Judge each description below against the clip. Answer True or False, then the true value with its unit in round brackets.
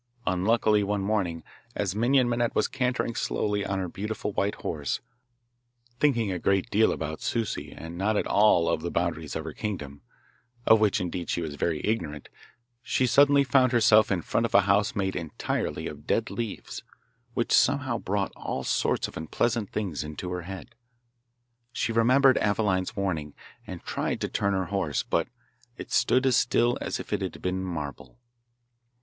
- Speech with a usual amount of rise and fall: True (4.6 semitones)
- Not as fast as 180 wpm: True (170 wpm)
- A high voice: False (100 Hz)